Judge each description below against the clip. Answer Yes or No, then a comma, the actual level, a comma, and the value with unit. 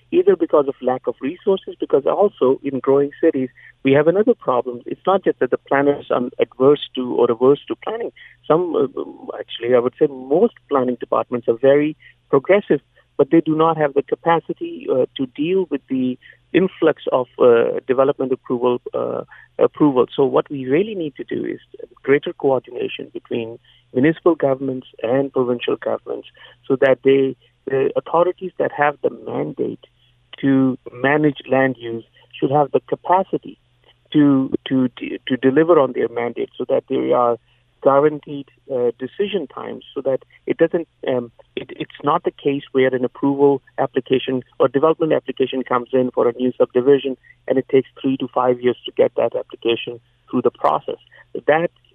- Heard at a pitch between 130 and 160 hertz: Yes, medium, 140 Hz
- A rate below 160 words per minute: No, average, 165 wpm